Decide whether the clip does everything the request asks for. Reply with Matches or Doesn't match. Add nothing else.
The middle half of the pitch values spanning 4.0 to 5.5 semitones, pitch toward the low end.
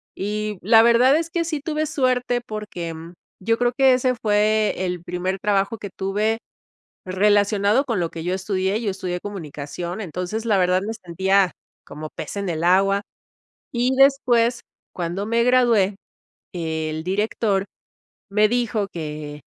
Doesn't match